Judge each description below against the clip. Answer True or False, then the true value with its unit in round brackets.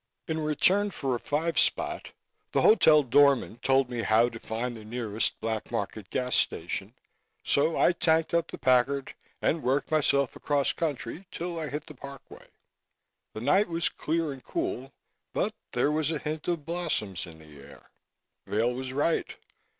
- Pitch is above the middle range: False (140 Hz)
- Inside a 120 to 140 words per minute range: False (170 wpm)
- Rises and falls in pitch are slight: False (4.9 semitones)